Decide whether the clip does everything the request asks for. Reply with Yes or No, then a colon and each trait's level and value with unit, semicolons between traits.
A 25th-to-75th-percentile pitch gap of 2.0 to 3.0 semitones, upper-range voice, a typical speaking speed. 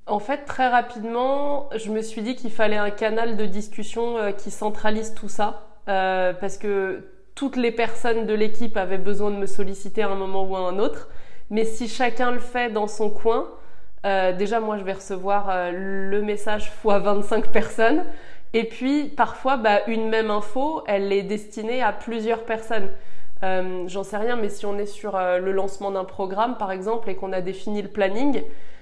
Yes: narrow, 2.5 semitones; high, 210 Hz; average, 195 wpm